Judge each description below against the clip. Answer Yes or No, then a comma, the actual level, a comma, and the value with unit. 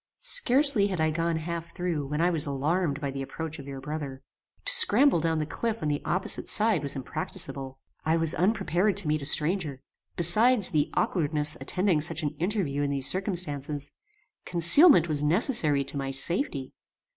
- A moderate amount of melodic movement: Yes, average, 4.6 semitones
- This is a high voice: No, medium, 160 Hz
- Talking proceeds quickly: No, average, 175 wpm